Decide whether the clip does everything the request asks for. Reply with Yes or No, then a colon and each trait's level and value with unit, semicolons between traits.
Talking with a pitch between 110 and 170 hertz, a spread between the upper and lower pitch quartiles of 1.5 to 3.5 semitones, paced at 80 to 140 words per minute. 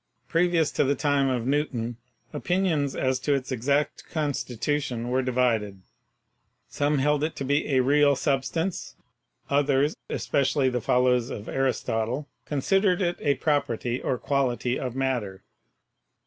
Yes: low, 135 Hz; average, 2.8 semitones; slow, 135 wpm